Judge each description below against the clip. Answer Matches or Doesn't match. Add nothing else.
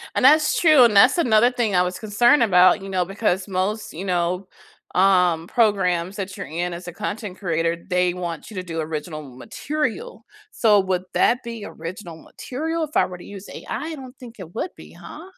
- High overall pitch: Matches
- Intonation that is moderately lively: Matches